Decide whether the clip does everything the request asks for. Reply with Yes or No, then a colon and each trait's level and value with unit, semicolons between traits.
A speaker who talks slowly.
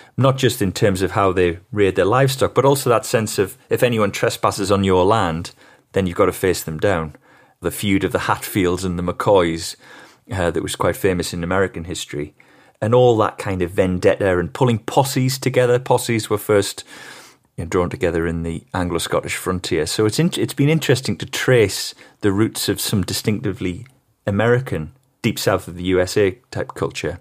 No: average, 190 wpm